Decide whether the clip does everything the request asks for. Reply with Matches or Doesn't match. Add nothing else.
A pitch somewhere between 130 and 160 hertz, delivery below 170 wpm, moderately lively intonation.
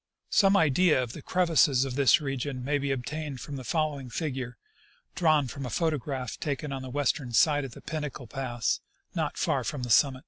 Doesn't match